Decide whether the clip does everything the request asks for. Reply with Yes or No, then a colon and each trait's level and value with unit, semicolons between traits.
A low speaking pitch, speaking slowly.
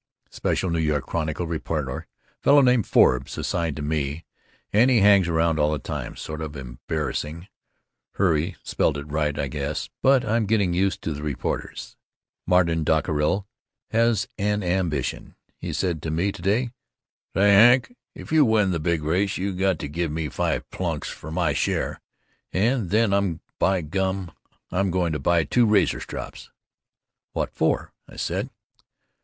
No: very low, 85 Hz; average, 160 wpm